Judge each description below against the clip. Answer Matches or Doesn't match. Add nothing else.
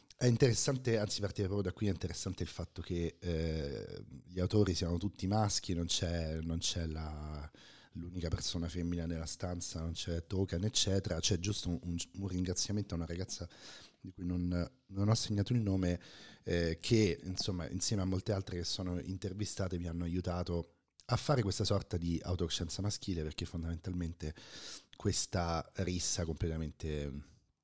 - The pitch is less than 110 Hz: Matches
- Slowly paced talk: Doesn't match